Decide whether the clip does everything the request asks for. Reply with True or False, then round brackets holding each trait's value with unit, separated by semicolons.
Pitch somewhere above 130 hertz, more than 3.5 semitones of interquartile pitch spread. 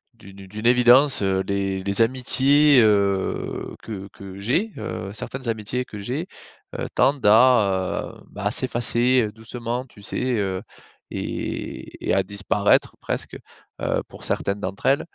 False (110 Hz; 4.1 semitones)